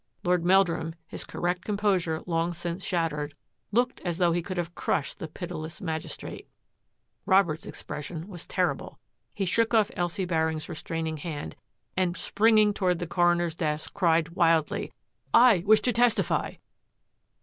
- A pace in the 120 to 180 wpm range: Yes, average, 150 wpm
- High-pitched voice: No, medium, 175 Hz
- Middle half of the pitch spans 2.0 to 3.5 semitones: Yes, average, 2.9 semitones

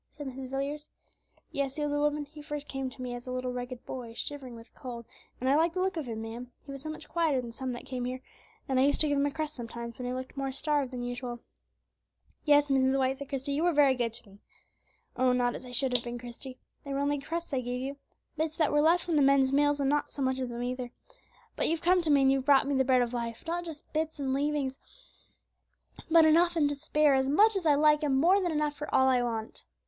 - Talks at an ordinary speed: No, fast, 265 wpm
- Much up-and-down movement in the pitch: No, average, 2.9 semitones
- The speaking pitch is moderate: No, very high, 275 Hz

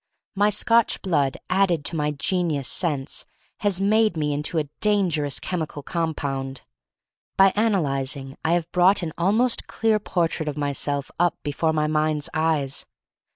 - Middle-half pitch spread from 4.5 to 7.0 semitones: Yes, average, 4.8 semitones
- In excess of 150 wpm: No, average, 145 wpm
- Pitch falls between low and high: Yes, medium, 160 Hz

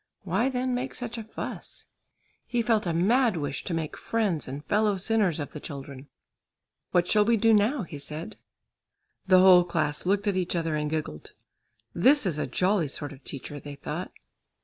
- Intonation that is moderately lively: No, wide, 6.5 semitones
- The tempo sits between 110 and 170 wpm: No, average, 185 wpm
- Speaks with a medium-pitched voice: Yes, medium, 180 Hz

